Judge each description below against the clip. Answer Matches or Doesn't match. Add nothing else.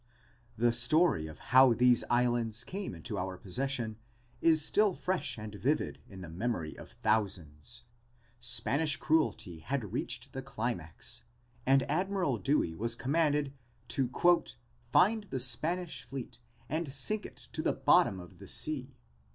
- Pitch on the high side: Doesn't match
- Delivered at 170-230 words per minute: Doesn't match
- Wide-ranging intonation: Matches